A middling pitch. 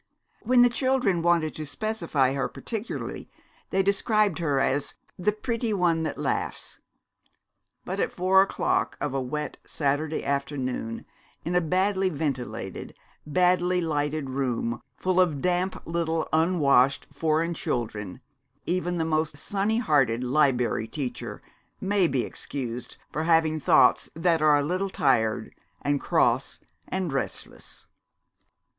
Yes: medium, 160 Hz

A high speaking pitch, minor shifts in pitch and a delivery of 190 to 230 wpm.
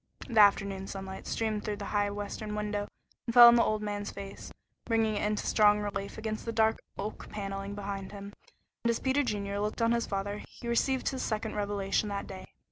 Yes: high, 210 Hz; narrow, 1.7 semitones; fast, 205 wpm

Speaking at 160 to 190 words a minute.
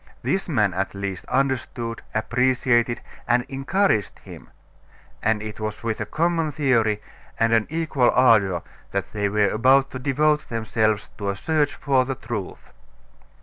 No: average, 150 wpm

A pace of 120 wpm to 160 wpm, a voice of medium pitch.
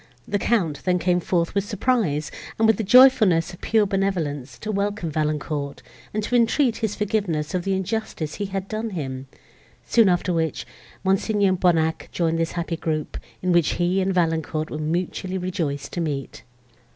No: average, 170 wpm; medium, 180 Hz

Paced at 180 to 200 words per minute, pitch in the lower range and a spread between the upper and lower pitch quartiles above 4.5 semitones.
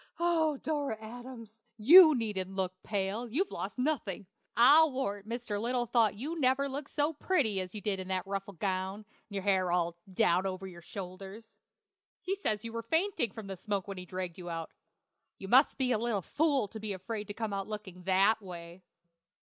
No: average, 190 wpm; high, 210 Hz; average, 4.9 semitones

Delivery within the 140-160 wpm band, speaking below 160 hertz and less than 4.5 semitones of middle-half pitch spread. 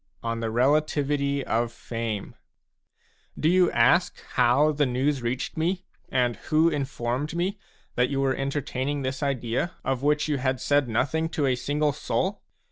Yes: average, 155 wpm; medium, 140 Hz; average, 3.4 semitones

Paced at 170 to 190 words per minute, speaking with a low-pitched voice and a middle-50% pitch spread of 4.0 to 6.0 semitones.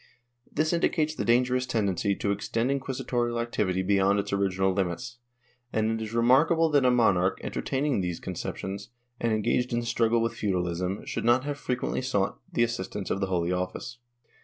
Yes: average, 175 wpm; low, 115 Hz; average, 4.5 semitones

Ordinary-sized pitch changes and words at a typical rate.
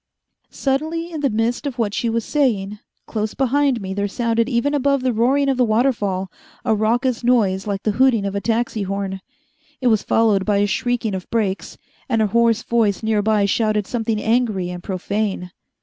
Yes: average, 3.4 semitones; average, 190 wpm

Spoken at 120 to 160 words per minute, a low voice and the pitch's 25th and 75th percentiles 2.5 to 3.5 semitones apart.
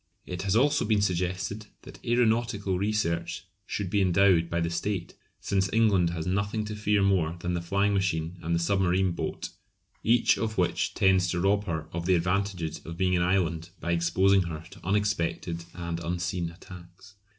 No: average, 175 wpm; very low, 90 Hz; average, 2.9 semitones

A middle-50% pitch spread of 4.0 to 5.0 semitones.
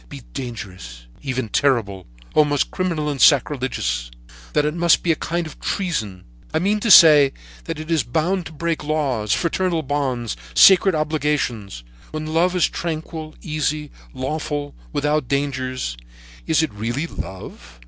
Yes: average, 4.4 semitones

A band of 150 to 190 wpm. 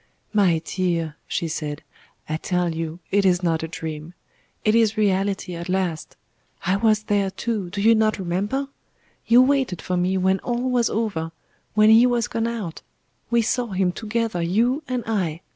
Yes: average, 175 wpm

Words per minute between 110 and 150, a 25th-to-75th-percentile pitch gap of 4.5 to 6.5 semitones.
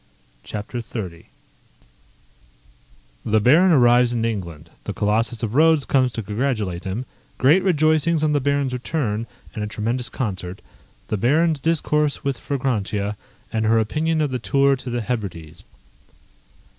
Yes: average, 140 wpm; average, 5.2 semitones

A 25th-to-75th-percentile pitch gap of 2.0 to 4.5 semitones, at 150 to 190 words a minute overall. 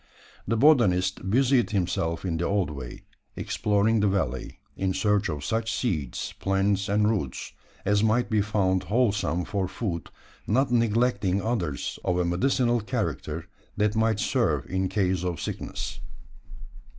No: average, 3.6 semitones; average, 140 wpm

